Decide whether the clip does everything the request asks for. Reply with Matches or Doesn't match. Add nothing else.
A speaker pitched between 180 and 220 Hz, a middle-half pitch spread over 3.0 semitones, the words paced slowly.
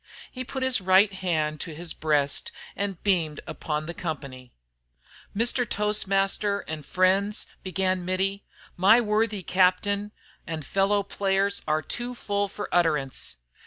Matches